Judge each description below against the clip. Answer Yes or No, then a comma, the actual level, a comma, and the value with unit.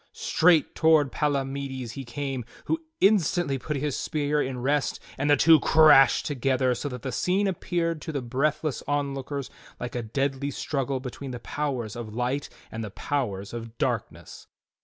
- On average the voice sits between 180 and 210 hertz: No, medium, 140 Hz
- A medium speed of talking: Yes, average, 165 wpm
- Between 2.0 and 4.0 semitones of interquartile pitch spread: Yes, average, 3.0 semitones